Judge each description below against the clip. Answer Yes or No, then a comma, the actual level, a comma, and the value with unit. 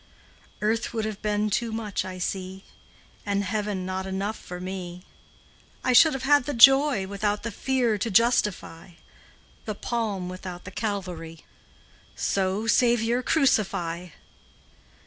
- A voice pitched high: Yes, high, 205 Hz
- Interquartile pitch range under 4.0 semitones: Yes, average, 3.6 semitones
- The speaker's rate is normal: No, slow, 130 wpm